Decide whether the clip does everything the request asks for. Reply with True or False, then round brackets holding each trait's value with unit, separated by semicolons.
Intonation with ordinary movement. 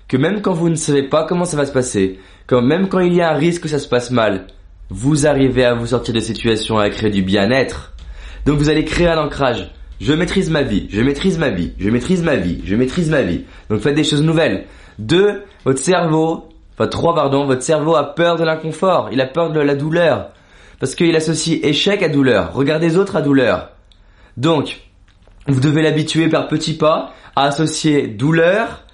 False (6.2 semitones)